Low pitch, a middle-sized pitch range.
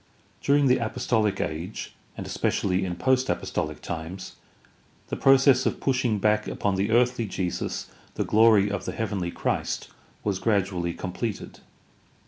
Yes: low, 105 Hz; average, 4.7 semitones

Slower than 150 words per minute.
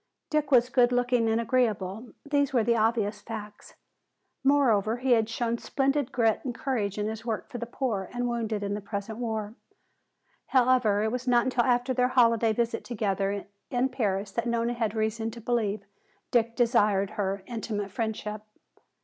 No: average, 165 wpm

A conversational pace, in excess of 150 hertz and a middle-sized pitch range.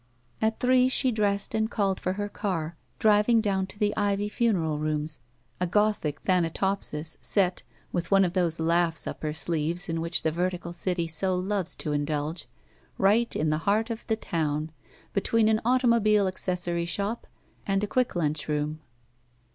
Yes: average, 170 wpm; medium, 185 Hz; average, 4.3 semitones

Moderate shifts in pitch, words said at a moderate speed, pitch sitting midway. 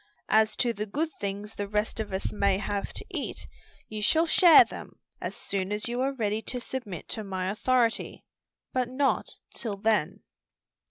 No: average, 3.6 semitones; average, 175 wpm; high, 215 Hz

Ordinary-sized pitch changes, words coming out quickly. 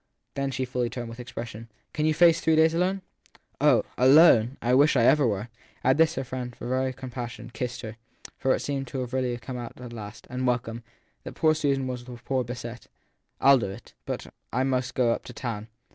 No: narrow, 2.2 semitones; fast, 235 wpm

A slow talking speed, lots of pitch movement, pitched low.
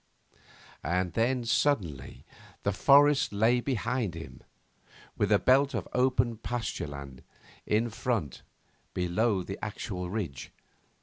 Yes: slow, 115 wpm; wide, 5.7 semitones; low, 110 Hz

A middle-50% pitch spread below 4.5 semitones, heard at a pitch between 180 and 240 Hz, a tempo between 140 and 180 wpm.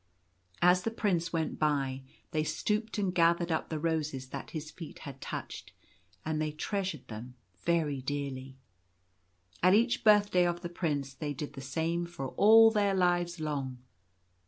No: average, 4.0 semitones; medium, 160 Hz; average, 160 wpm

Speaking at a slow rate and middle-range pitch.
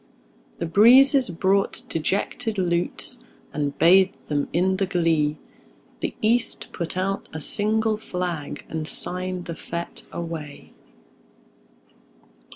Yes: slow, 110 wpm; medium, 180 Hz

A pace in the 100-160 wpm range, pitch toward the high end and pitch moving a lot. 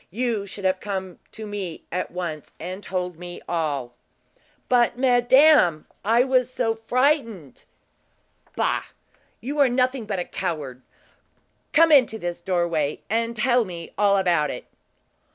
Yes: slow, 135 wpm; high, 200 Hz; wide, 5.8 semitones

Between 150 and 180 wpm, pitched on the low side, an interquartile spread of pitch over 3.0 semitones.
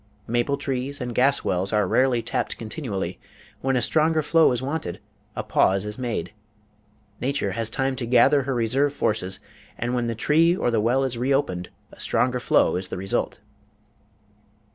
Yes: average, 170 wpm; low, 125 Hz; average, 4.1 semitones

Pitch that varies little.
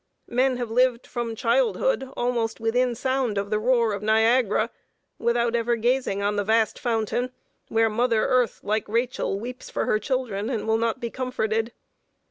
Yes: narrow, 2.3 semitones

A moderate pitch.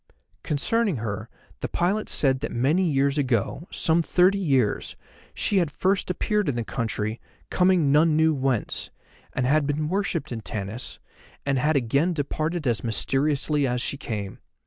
Yes: medium, 145 Hz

